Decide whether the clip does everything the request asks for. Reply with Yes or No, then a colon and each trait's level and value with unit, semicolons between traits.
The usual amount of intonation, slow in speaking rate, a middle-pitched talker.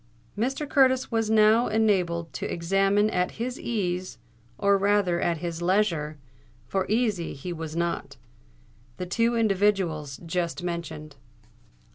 Yes: average, 4.2 semitones; slow, 115 wpm; medium, 180 Hz